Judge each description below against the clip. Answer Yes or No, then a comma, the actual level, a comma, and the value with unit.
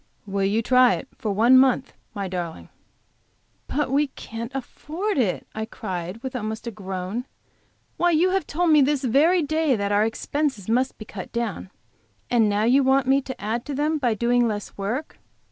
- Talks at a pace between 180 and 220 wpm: Yes, average, 185 wpm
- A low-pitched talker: No, high, 245 Hz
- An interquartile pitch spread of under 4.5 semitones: No, average, 4.9 semitones